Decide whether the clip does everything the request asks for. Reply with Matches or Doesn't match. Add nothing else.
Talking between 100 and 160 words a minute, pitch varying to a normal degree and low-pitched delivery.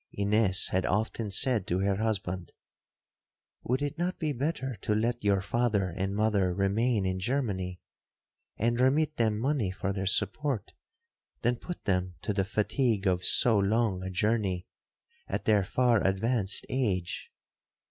Matches